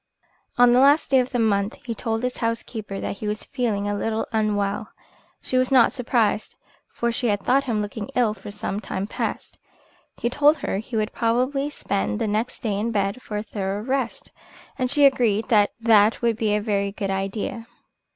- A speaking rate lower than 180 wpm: No, average, 200 wpm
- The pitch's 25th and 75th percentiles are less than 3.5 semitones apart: Yes, average, 3.1 semitones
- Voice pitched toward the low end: No, high, 225 Hz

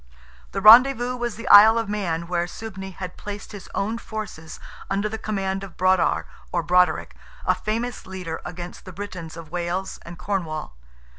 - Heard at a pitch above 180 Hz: Yes, high, 190 Hz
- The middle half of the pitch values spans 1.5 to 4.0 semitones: Yes, average, 3.4 semitones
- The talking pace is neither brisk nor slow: Yes, average, 165 wpm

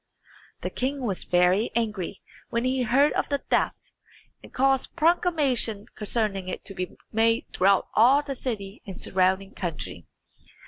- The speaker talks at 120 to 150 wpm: Yes, average, 145 wpm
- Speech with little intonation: No, average, 5.3 semitones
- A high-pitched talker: Yes, high, 225 Hz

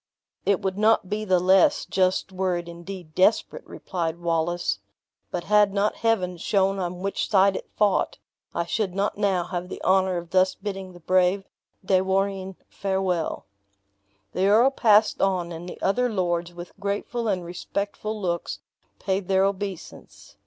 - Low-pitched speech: No, high, 190 Hz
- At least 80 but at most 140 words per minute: No, average, 160 wpm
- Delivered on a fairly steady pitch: Yes, narrow, 2.1 semitones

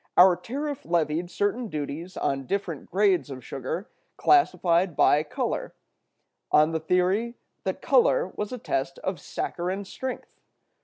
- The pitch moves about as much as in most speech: No, wide, 6.4 semitones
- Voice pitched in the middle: Yes, medium, 180 Hz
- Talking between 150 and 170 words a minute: No, slow, 135 wpm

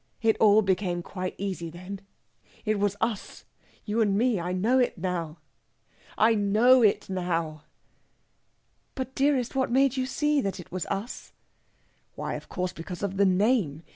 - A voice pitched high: Yes, high, 200 Hz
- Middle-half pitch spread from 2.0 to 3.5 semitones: No, average, 4.5 semitones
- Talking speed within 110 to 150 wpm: No, average, 160 wpm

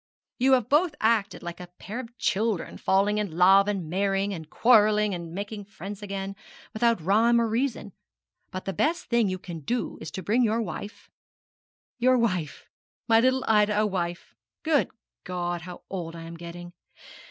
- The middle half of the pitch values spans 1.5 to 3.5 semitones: No, average, 4.3 semitones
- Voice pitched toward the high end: Yes, high, 205 Hz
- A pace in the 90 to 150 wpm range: No, average, 175 wpm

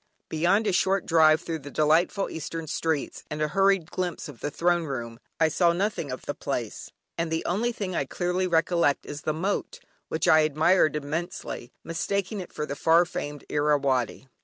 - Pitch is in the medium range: Yes, medium, 160 Hz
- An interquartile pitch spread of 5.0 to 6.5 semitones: No, average, 3.3 semitones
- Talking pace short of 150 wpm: No, average, 185 wpm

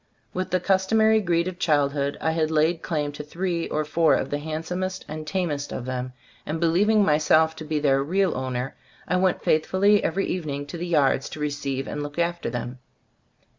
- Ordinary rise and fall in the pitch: Yes, average, 3.6 semitones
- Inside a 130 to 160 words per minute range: No, average, 195 wpm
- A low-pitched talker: No, medium, 155 Hz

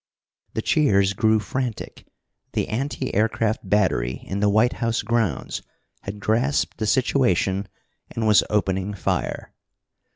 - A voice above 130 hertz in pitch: No, low, 105 Hz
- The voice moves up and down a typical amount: Yes, average, 3.0 semitones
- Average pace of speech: No, slow, 125 wpm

